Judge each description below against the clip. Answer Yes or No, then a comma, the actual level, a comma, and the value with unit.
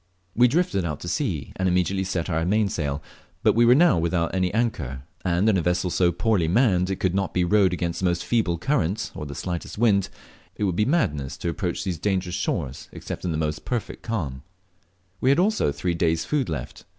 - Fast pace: Yes, fast, 220 wpm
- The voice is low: Yes, very low, 90 Hz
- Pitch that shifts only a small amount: No, average, 4.2 semitones